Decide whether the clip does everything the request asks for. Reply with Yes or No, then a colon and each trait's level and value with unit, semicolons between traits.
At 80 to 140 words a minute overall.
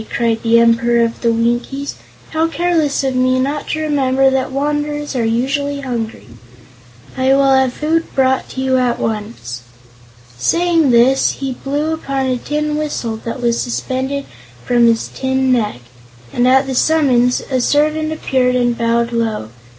No: average, 155 wpm